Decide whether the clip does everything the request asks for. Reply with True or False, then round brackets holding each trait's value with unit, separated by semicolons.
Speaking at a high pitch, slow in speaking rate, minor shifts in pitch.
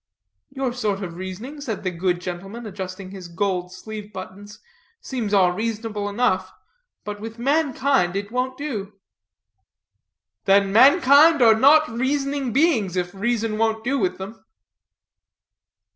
False (215 Hz; 130 wpm; 5.0 semitones)